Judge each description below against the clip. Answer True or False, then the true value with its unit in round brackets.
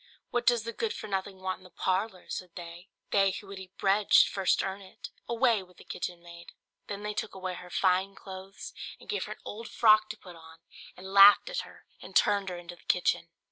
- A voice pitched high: True (195 Hz)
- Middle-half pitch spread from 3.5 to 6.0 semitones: False (2.4 semitones)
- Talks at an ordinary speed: False (235 wpm)